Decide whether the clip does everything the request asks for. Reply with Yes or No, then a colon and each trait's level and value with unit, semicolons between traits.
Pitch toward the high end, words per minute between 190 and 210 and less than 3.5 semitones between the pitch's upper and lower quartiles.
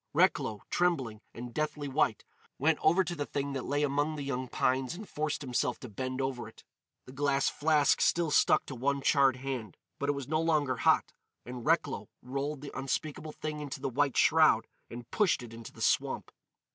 No: medium, 140 Hz; average, 195 wpm; average, 2.8 semitones